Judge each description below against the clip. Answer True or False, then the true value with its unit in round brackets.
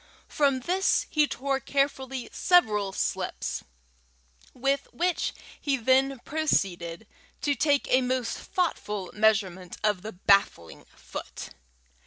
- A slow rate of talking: True (110 wpm)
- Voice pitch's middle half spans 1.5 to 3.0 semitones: False (5.4 semitones)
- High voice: True (260 Hz)